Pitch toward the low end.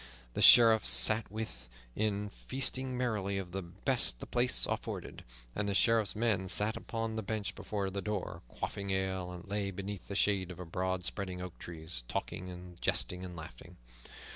Yes: low, 100 Hz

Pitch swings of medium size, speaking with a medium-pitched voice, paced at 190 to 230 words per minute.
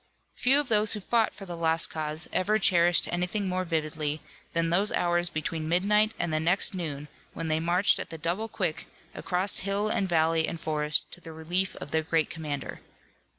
Yes: average, 3.2 semitones; medium, 170 Hz; average, 195 wpm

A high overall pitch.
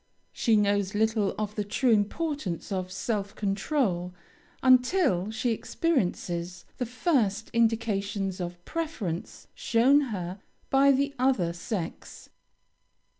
Yes: high, 210 Hz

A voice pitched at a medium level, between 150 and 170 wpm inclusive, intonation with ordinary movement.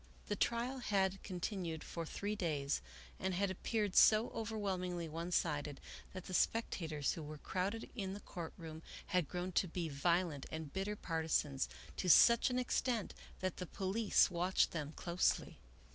Yes: medium, 180 Hz; average, 160 wpm; average, 3.8 semitones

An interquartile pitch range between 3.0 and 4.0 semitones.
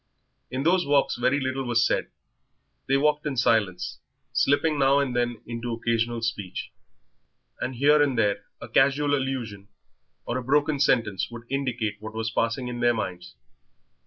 Yes: average, 3.4 semitones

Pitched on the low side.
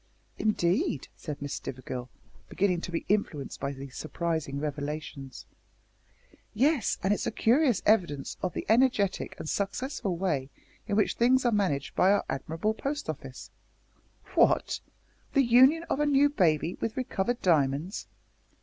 No: high, 190 Hz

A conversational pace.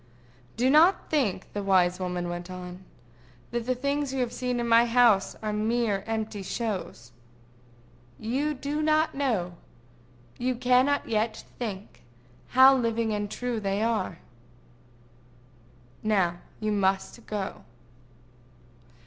No: slow, 120 wpm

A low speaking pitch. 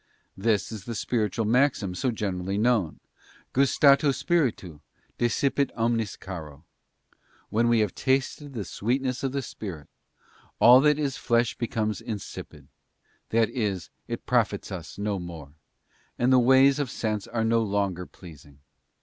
Yes: low, 115 Hz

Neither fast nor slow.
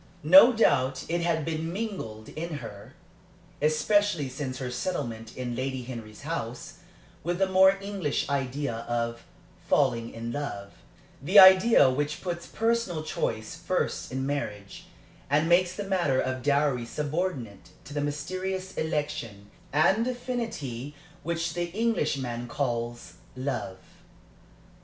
No: slow, 125 wpm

